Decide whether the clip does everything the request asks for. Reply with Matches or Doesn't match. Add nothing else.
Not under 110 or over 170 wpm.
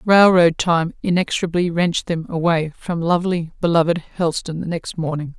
Matches